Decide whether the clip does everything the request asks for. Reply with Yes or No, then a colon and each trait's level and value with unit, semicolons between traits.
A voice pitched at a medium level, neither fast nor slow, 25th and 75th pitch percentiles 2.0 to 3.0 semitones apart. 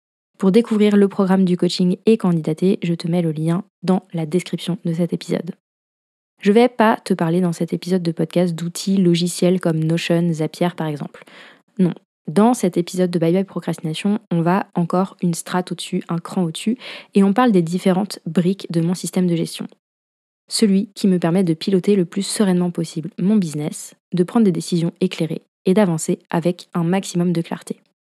Yes: medium, 180 Hz; average, 190 wpm; narrow, 2.4 semitones